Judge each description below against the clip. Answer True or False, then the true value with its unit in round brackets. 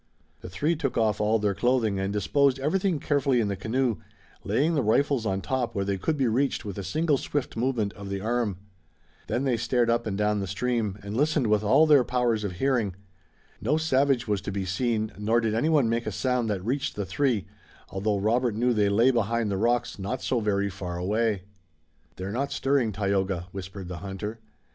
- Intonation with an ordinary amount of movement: True (4.3 semitones)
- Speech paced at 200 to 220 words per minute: True (205 wpm)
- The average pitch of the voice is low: True (115 Hz)